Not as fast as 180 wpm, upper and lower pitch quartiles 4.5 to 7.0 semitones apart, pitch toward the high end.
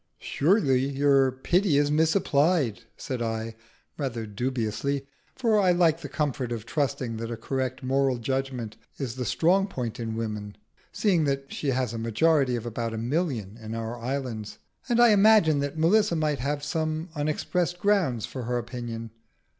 No: average, 160 wpm; average, 5.2 semitones; low, 135 Hz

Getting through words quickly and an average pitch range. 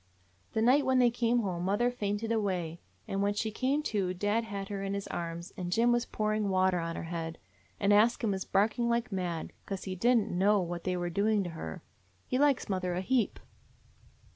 Yes: fast, 215 wpm; average, 4.0 semitones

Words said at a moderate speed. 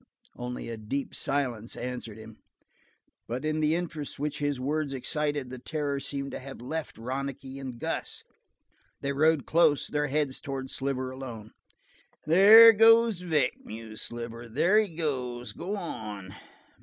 Yes: average, 145 wpm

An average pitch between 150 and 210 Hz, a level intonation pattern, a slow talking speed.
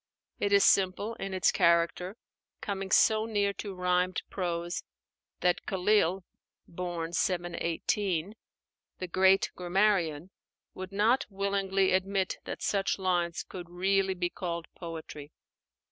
Yes: medium, 185 Hz; narrow, 2.1 semitones; slow, 115 wpm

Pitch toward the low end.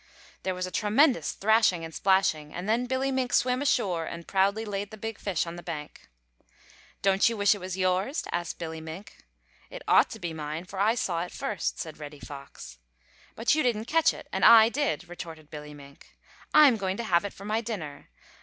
No: high, 195 Hz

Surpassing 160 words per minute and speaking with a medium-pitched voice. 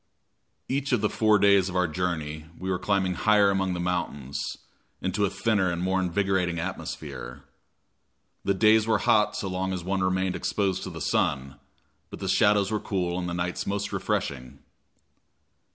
No: average, 170 wpm; very low, 95 Hz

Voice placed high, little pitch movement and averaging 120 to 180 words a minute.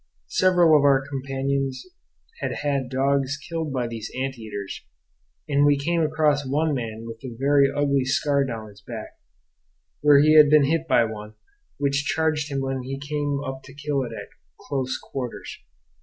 No: medium, 140 Hz; narrow, 2.1 semitones; average, 170 wpm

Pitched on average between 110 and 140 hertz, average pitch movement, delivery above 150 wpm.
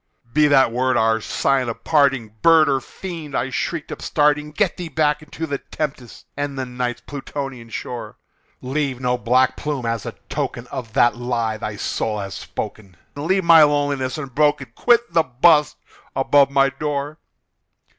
Yes: low, 135 Hz; average, 3.4 semitones; average, 160 wpm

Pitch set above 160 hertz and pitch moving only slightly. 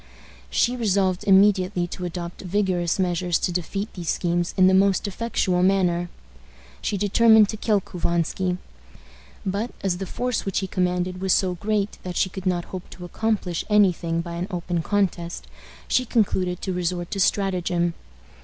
Yes: medium, 185 Hz; narrow, 2.2 semitones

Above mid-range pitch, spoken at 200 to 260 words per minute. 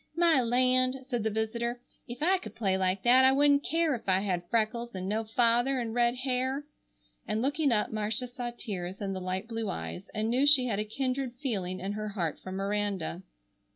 Yes: high, 230 Hz; fast, 205 wpm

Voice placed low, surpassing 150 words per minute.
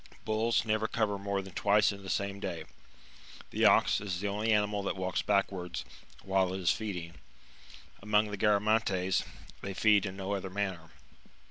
Yes: low, 100 Hz; average, 170 wpm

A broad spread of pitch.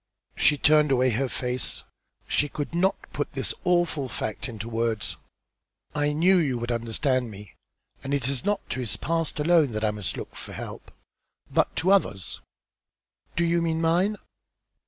Yes: wide, 5.9 semitones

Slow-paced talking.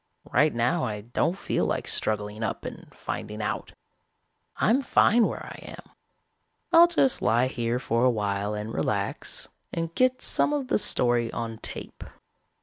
No: average, 155 wpm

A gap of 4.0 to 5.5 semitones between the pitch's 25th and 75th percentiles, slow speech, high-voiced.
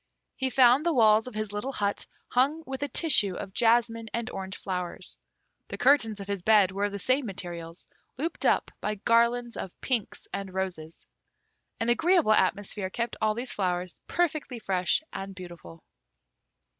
No: average, 4.7 semitones; average, 165 wpm; high, 215 Hz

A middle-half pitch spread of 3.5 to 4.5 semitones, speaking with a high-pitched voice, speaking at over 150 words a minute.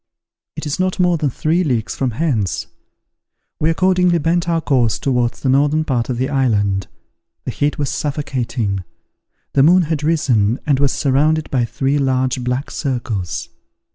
No: average, 4.1 semitones; low, 135 Hz; average, 160 wpm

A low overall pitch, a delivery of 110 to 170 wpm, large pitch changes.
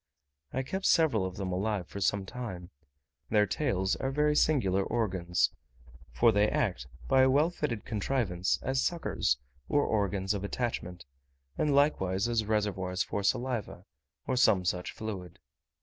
Yes: low, 105 Hz; average, 150 wpm; wide, 5.7 semitones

